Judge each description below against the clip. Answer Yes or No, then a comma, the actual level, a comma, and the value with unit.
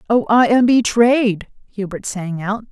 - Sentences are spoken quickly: No, average, 155 wpm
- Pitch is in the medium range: No, high, 215 Hz